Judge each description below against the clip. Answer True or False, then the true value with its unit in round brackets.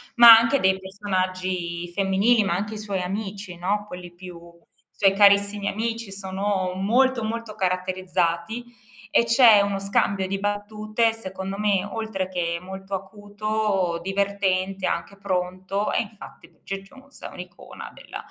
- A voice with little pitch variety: True (2.3 semitones)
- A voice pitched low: False (195 Hz)